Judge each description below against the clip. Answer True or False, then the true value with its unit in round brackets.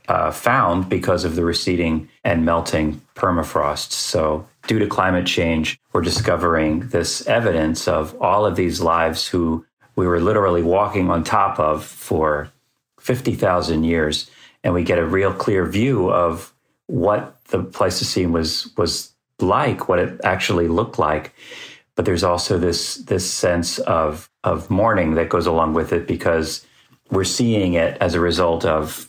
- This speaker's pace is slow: False (160 wpm)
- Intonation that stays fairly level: True (1.7 semitones)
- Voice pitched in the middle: False (85 Hz)